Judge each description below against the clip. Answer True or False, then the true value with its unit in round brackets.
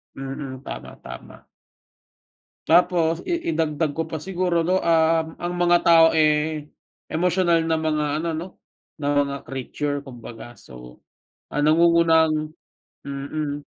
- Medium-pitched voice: True (160 Hz)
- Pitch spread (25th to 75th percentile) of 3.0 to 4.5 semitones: False (2.6 semitones)